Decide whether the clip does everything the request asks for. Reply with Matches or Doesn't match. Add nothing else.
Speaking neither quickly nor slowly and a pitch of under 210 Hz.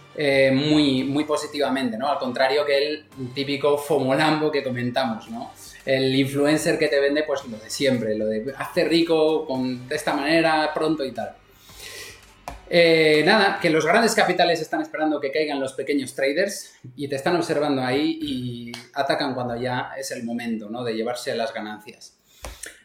Matches